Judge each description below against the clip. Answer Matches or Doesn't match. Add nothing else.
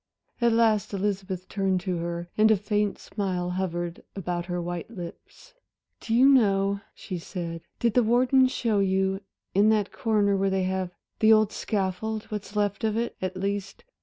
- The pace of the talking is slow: Doesn't match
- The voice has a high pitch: Matches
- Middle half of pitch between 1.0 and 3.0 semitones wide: Matches